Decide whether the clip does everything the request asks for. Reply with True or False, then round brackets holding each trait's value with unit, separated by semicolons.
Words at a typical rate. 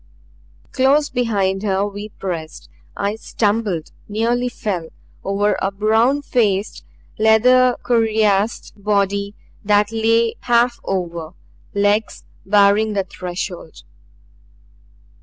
False (95 wpm)